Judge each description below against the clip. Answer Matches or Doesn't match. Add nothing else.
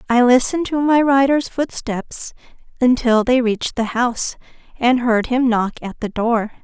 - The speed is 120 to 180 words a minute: Matches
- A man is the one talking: Doesn't match